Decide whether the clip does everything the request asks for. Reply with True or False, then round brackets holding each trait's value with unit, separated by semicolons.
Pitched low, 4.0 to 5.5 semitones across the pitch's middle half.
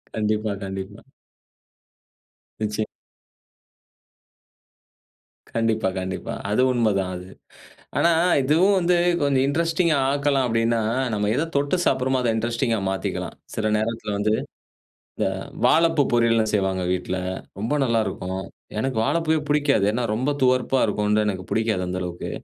True (115 Hz; 4.9 semitones)